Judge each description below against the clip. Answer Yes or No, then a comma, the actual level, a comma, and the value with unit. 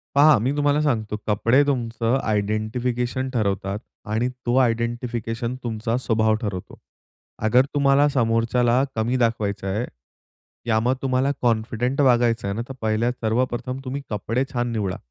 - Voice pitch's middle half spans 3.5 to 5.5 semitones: No, narrow, 2.6 semitones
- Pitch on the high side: No, low, 120 Hz